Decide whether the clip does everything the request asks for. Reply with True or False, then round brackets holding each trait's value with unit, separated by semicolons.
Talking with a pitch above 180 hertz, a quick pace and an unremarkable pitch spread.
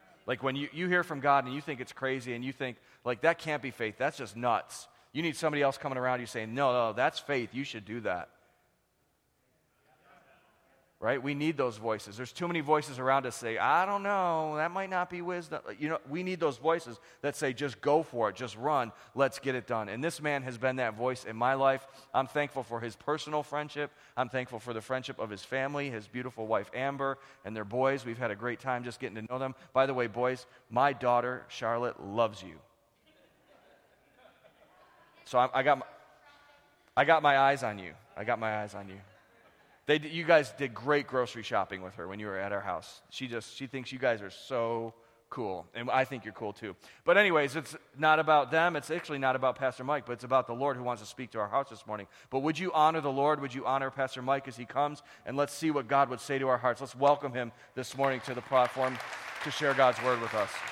False (130 Hz; 235 wpm; 3.2 semitones)